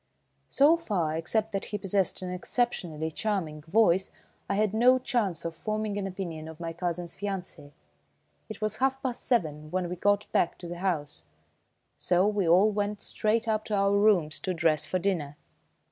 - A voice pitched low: No, high, 190 Hz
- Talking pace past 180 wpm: No, average, 175 wpm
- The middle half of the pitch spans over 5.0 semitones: No, average, 4.2 semitones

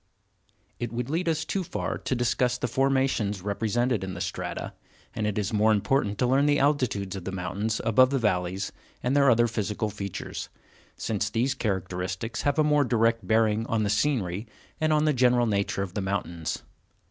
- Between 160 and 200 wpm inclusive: Yes, average, 185 wpm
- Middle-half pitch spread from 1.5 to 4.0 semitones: No, average, 4.6 semitones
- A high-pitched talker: No, low, 115 Hz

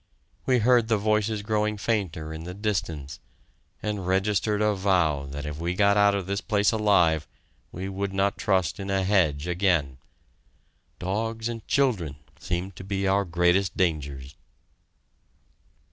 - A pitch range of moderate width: Yes, average, 3.6 semitones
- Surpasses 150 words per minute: No, average, 145 wpm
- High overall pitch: No, very low, 95 Hz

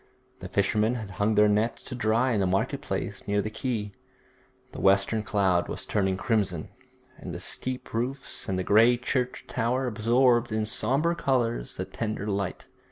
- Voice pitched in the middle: No, low, 110 Hz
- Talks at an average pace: Yes, average, 165 wpm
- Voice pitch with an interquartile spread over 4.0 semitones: No, average, 3.3 semitones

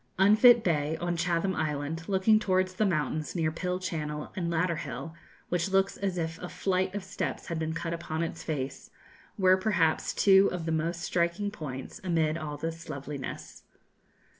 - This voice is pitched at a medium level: Yes, medium, 170 Hz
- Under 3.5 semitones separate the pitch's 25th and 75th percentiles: Yes, average, 3.0 semitones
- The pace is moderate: Yes, average, 170 wpm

